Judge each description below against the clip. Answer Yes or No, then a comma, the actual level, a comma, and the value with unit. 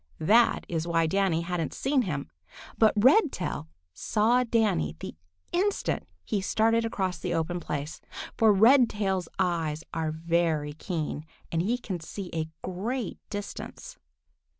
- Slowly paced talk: Yes, slow, 130 wpm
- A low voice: No, medium, 185 Hz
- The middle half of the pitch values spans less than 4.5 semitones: No, wide, 5.5 semitones